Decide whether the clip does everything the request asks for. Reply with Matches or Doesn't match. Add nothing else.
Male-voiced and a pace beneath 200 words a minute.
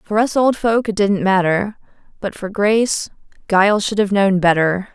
Doesn't match